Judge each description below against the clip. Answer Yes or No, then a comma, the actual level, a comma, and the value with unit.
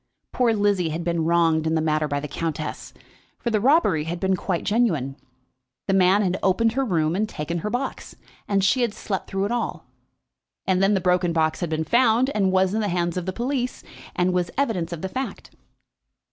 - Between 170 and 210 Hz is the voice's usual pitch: Yes, medium, 185 Hz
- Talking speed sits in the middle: No, fast, 210 wpm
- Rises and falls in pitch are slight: No, average, 4.5 semitones